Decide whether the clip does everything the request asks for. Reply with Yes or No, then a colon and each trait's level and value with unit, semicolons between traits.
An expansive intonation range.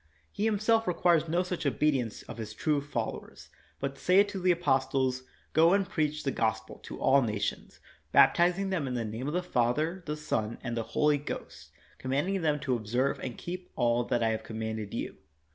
Yes: wide, 6.6 semitones